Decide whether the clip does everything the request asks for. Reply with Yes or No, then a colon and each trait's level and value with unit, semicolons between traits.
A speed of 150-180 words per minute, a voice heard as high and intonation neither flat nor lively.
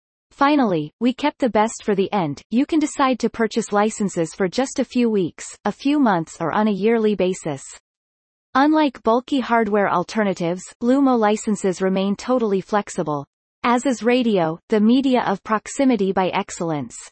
Yes: average, 160 wpm; high, 215 Hz; average, 4.7 semitones